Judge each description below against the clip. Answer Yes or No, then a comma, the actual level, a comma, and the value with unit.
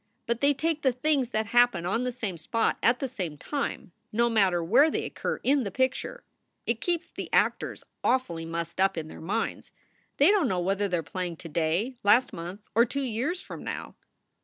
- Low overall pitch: No, high, 230 Hz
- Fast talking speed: Yes, fast, 210 wpm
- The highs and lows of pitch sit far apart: Yes, wide, 6.5 semitones